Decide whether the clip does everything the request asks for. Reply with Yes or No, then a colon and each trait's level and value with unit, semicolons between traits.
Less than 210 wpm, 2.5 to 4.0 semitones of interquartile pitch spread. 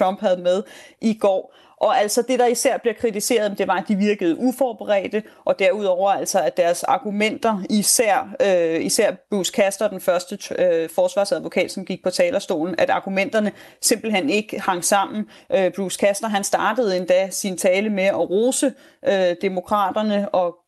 Yes: average, 165 wpm; average, 3.6 semitones